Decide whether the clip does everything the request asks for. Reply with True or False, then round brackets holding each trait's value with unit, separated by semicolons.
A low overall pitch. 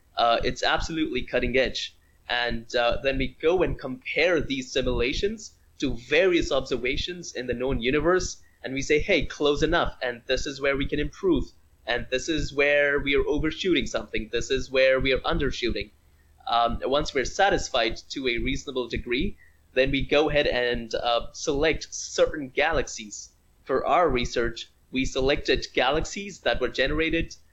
True (130 Hz)